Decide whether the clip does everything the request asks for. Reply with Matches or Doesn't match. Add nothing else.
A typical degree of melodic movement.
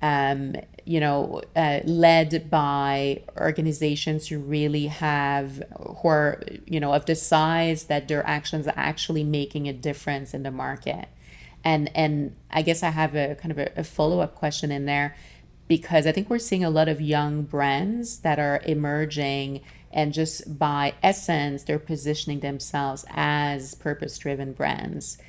Doesn't match